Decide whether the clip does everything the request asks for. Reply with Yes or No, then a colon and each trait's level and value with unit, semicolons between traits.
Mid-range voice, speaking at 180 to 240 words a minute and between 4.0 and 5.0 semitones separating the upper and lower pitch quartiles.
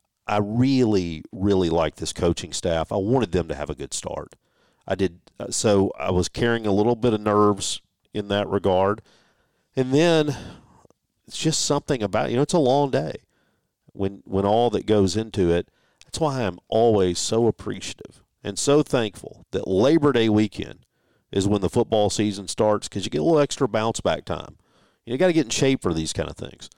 No: low, 105 Hz; average, 200 wpm; average, 4.4 semitones